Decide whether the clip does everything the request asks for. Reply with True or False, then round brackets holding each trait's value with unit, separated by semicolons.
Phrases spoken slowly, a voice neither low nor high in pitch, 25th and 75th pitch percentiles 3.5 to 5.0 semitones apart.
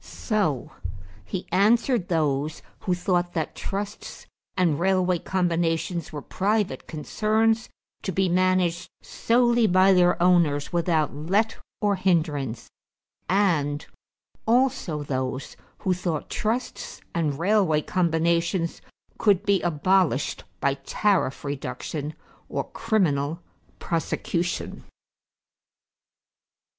True (95 wpm; 175 Hz; 4.2 semitones)